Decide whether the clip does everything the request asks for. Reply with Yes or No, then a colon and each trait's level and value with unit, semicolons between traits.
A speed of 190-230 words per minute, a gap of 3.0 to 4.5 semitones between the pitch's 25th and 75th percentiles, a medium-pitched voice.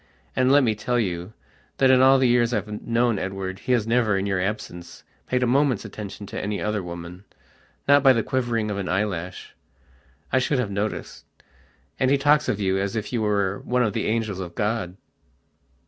No: average, 195 wpm; average, 4.2 semitones; low, 110 Hz